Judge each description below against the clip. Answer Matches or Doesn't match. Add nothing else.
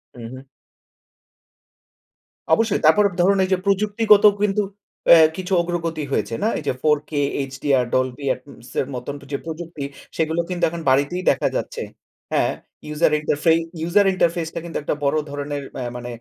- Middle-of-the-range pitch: Matches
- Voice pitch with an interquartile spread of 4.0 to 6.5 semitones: Matches